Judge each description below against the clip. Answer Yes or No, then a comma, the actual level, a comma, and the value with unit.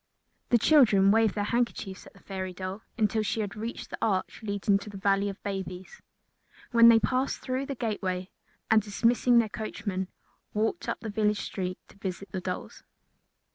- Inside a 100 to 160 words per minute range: No, average, 175 wpm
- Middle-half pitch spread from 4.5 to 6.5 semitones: No, average, 2.8 semitones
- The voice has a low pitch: No, high, 210 Hz